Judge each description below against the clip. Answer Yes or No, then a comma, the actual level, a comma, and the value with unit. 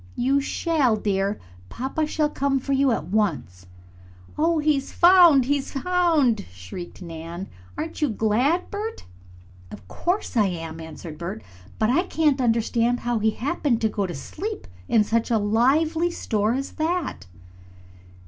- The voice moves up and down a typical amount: No, wide, 7.0 semitones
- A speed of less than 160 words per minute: Yes, average, 150 wpm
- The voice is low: No, high, 245 Hz